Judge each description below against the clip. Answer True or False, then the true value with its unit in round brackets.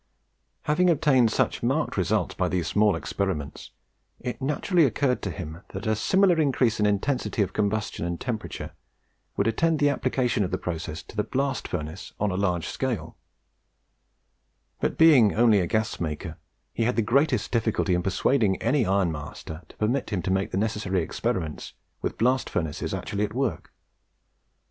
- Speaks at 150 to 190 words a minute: True (165 wpm)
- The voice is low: True (105 Hz)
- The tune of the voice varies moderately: False (5.8 semitones)